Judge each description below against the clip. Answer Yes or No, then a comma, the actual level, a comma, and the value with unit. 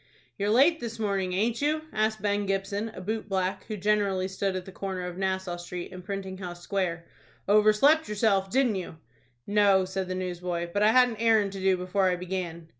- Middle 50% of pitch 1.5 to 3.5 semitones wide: Yes, narrow, 2.5 semitones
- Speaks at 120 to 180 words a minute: No, average, 200 wpm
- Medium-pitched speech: No, high, 195 Hz